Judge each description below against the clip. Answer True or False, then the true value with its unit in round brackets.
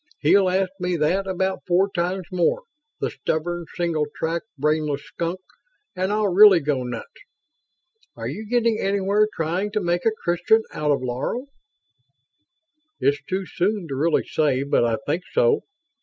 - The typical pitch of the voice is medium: True (175 Hz)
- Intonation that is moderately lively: True (4.4 semitones)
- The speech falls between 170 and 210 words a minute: False (155 wpm)